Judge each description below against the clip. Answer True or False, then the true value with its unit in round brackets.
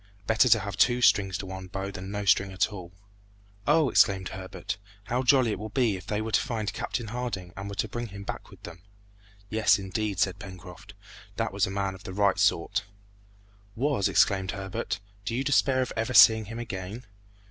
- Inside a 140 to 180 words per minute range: False (200 wpm)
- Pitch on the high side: False (100 Hz)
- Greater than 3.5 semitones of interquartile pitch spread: False (3.1 semitones)